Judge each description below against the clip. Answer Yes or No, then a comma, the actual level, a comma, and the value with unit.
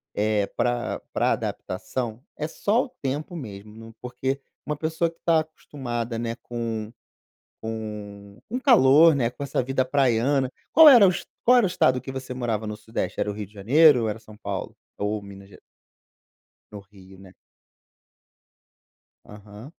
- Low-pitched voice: Yes, low, 120 Hz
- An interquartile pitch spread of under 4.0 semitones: No, average, 5.2 semitones